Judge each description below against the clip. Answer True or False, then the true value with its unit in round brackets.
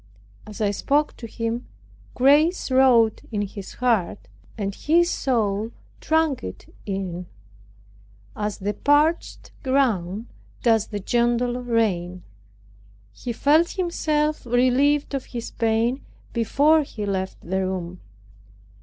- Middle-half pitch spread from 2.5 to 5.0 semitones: False (5.4 semitones)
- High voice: True (235 Hz)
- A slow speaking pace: True (115 wpm)